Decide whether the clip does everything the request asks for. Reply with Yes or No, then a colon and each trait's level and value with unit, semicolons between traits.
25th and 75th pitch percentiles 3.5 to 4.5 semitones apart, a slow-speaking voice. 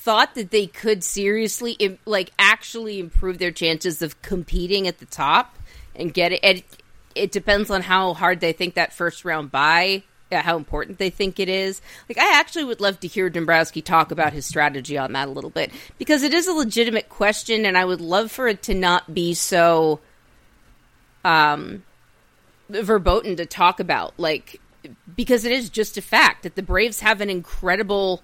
No: average, 3.9 semitones; average, 185 wpm